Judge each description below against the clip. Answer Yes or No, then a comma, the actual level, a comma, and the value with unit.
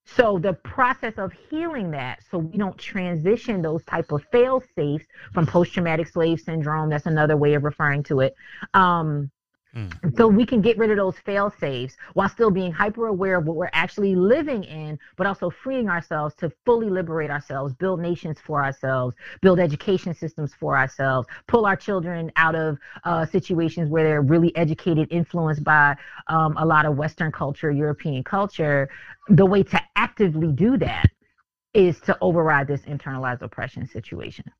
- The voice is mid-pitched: Yes, medium, 165 Hz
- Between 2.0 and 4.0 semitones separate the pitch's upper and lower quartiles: No, average, 4.6 semitones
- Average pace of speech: Yes, average, 170 wpm